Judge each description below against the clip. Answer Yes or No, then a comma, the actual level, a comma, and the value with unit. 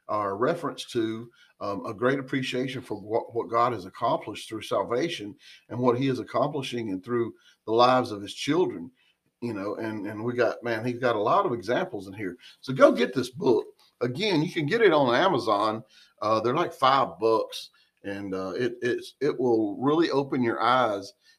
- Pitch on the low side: Yes, low, 125 Hz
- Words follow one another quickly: No, average, 195 wpm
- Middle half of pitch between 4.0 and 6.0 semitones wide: Yes, average, 4.6 semitones